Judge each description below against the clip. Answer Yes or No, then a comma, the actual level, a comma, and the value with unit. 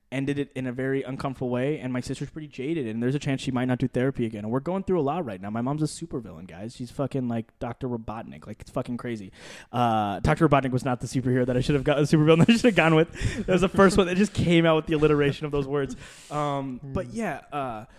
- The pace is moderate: No, fast, 275 wpm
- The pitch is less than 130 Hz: No, low, 135 Hz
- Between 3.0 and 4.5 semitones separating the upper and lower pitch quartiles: Yes, average, 3.6 semitones